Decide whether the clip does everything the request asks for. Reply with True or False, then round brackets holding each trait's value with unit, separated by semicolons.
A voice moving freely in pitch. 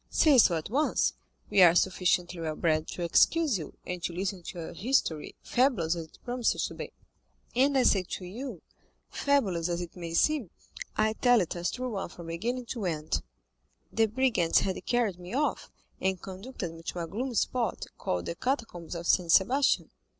True (6.4 semitones)